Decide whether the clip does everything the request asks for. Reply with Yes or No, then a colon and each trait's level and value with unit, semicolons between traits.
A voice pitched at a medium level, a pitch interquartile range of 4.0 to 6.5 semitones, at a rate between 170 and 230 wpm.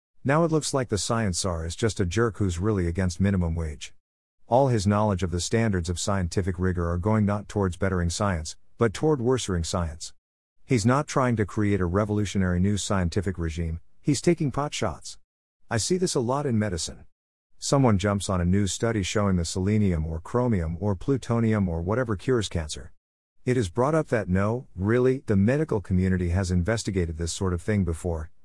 No: low, 100 Hz; average, 4.6 semitones; average, 190 wpm